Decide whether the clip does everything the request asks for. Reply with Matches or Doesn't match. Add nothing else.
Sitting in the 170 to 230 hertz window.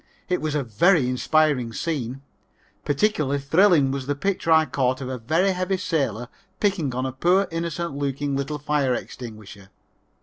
Doesn't match